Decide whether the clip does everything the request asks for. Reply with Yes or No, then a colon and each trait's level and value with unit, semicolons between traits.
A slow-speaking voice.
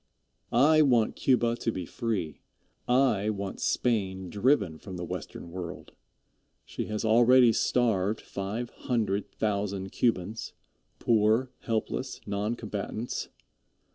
Yes: slow, 110 wpm